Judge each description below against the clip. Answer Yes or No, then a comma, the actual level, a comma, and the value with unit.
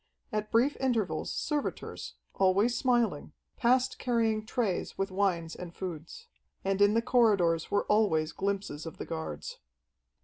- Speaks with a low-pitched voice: No, high, 205 Hz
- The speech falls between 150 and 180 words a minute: No, slow, 135 wpm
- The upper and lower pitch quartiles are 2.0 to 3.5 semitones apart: No, average, 5.1 semitones